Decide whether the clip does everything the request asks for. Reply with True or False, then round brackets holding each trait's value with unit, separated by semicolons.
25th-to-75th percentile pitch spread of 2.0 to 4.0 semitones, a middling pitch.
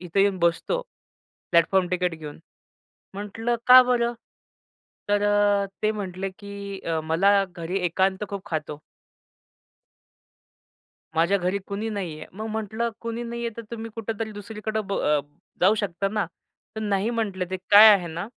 False (3.2 semitones; 200 Hz)